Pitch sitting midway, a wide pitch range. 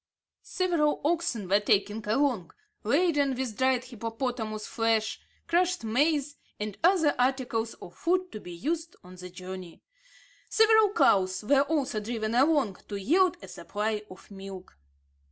No: high, 240 Hz; wide, 6.6 semitones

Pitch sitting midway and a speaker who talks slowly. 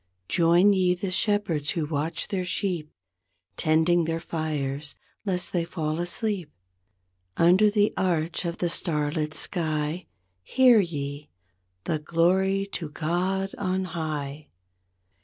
Yes: medium, 170 Hz; slow, 120 wpm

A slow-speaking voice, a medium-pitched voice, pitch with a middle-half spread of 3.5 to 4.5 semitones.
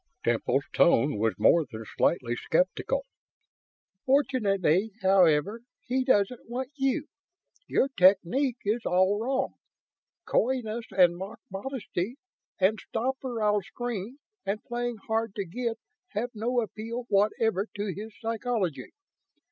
No: slow, 120 wpm; high, 220 Hz; average, 4.2 semitones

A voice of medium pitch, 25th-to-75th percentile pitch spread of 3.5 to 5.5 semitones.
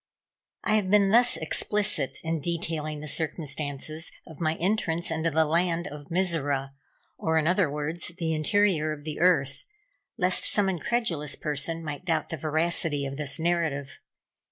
No: medium, 160 Hz; average, 2.8 semitones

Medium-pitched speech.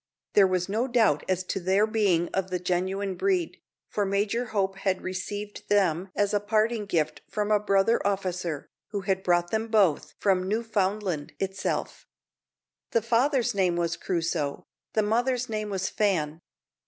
No: high, 195 Hz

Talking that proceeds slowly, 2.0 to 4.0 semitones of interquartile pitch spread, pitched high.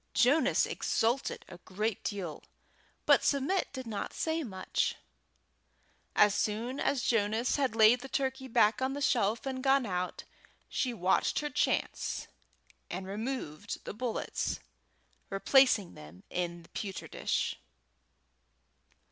No: slow, 125 wpm; average, 5.2 semitones; high, 230 Hz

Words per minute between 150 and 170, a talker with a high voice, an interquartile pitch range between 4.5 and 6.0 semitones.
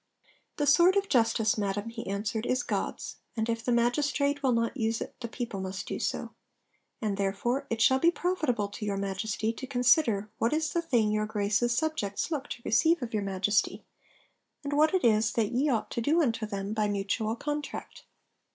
No: average, 195 wpm; high, 230 Hz; average, 5.1 semitones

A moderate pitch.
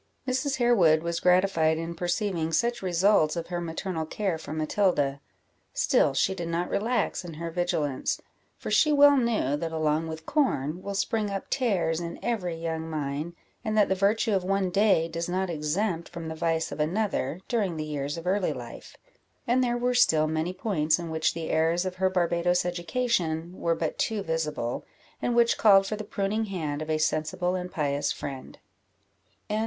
Yes: medium, 175 Hz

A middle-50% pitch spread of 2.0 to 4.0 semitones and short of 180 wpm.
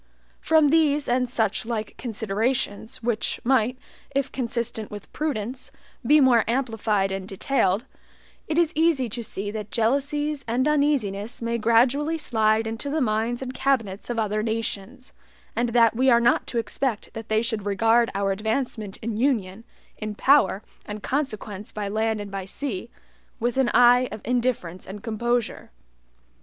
Yes: average, 3.5 semitones; average, 155 wpm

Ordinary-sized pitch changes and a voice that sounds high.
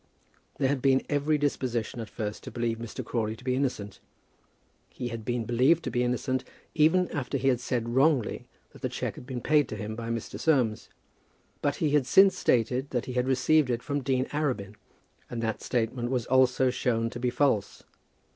No: average, 3.0 semitones; low, 125 Hz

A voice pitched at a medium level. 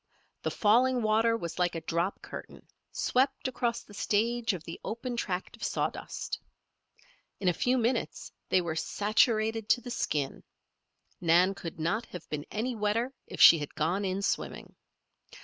No: high, 210 Hz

